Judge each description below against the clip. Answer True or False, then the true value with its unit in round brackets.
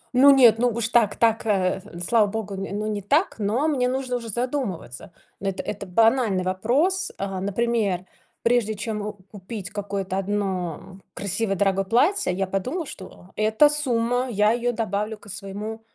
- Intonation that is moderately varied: True (3.6 semitones)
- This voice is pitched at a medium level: False (210 Hz)